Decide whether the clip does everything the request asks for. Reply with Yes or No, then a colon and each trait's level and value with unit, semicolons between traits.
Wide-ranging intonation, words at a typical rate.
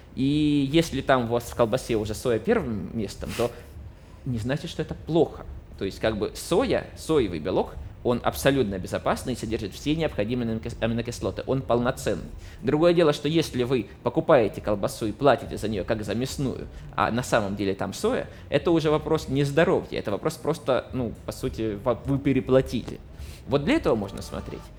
No: wide, 5.7 semitones; fast, 175 wpm